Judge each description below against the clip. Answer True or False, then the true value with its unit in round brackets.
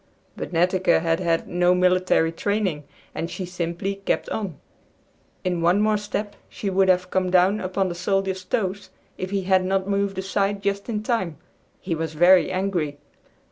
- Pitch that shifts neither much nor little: False (2.0 semitones)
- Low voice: False (185 Hz)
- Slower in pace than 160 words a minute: False (170 wpm)